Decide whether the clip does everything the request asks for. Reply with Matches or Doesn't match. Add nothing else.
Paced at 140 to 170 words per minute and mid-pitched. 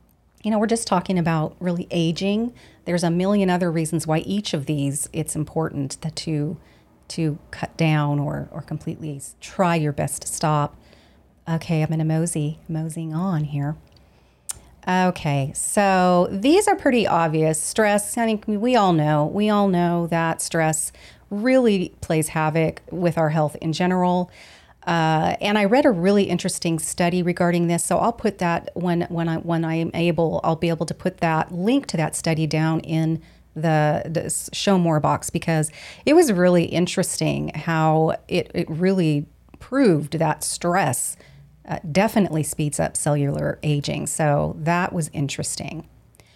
Matches